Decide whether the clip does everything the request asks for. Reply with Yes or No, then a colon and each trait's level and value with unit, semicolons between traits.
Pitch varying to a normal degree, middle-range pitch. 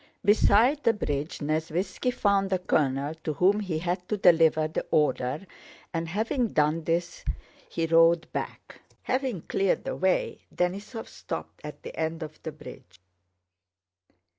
Yes: average, 4.3 semitones; medium, 170 Hz